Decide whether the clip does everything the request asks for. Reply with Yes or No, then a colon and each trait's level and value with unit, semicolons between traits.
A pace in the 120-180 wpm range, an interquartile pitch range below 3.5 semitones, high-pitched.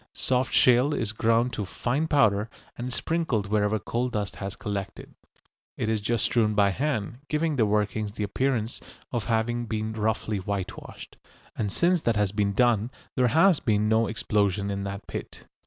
No: average, 170 wpm; average, 3.1 semitones; low, 110 Hz